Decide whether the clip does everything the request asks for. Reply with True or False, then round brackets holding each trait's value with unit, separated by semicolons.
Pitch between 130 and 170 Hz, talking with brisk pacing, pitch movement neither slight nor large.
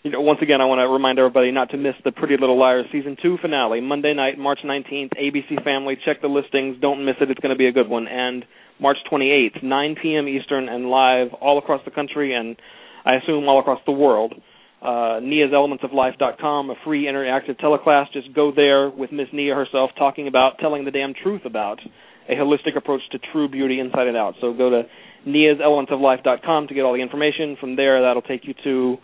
False (140 Hz; 230 wpm; 1.8 semitones)